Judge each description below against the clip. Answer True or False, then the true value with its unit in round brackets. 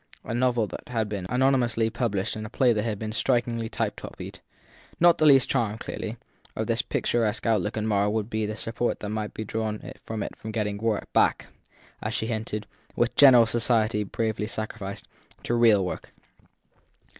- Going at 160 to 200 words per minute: True (180 wpm)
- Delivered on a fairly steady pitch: True (2.0 semitones)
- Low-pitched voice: True (110 Hz)